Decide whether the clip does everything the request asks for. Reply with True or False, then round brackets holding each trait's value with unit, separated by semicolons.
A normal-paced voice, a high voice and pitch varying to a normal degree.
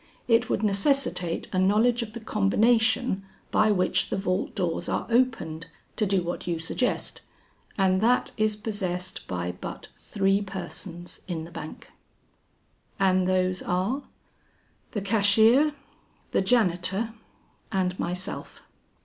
False (125 wpm; 195 Hz; 3.4 semitones)